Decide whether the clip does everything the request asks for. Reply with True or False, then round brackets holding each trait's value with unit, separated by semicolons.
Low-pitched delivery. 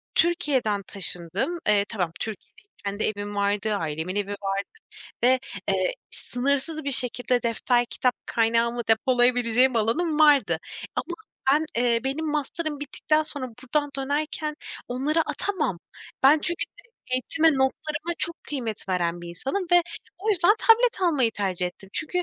False (255 Hz)